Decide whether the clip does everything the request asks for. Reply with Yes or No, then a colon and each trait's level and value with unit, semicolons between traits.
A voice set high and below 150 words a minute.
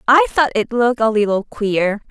No: high, 230 Hz; average, 200 wpm